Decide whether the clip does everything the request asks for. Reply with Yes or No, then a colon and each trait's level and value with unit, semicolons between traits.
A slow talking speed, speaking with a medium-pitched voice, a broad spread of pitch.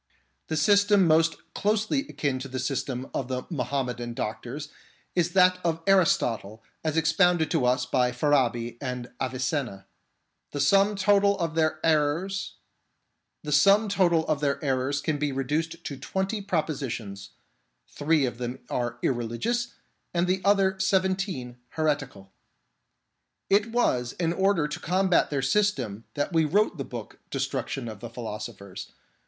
Yes: slow, 130 wpm; medium, 150 Hz; wide, 6.9 semitones